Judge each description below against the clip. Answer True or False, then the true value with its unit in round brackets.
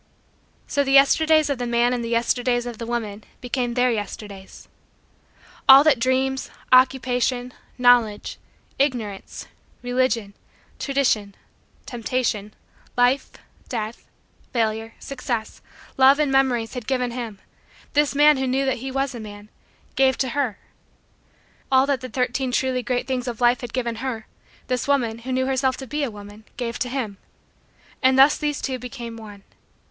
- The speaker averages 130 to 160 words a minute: True (150 wpm)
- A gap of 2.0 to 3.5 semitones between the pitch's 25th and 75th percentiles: True (2.5 semitones)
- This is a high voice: True (250 Hz)